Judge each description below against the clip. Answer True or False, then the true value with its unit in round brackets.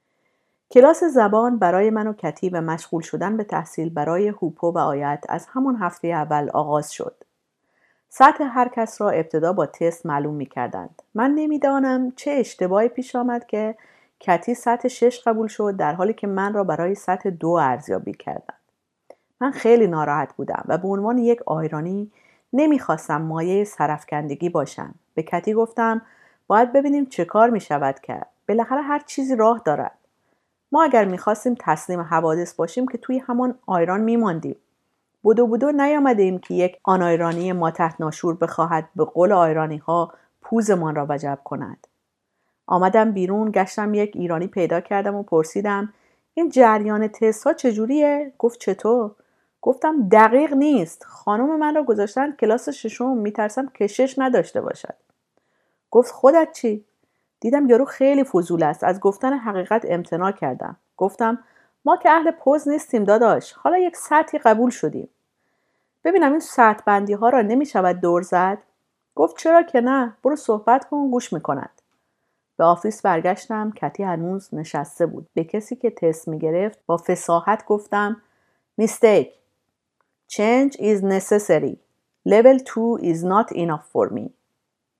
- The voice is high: True (210 Hz)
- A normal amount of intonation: False (6.5 semitones)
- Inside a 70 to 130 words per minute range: False (150 wpm)